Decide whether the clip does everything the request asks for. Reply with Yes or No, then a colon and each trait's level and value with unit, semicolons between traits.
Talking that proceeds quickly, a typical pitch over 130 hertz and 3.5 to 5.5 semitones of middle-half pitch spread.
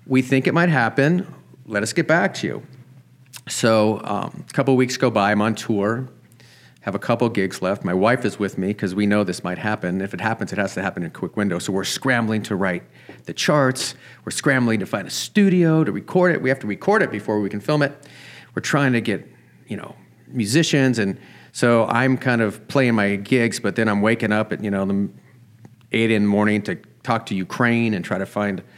No: fast, 230 wpm; low, 115 Hz; average, 4.2 semitones